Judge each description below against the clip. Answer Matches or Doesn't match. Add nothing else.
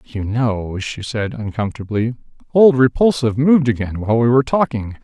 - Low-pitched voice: Matches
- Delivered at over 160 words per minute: Doesn't match